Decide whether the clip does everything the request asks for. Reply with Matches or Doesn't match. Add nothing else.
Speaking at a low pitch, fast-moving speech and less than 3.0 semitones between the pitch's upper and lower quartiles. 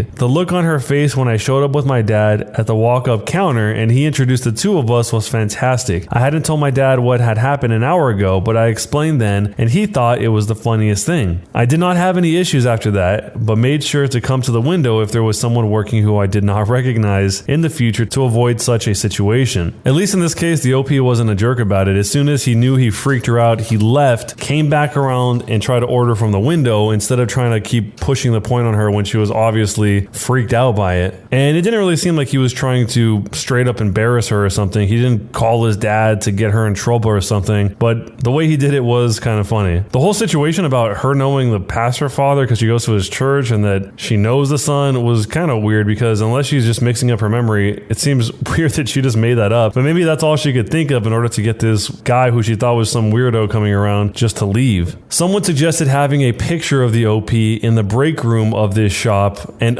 Doesn't match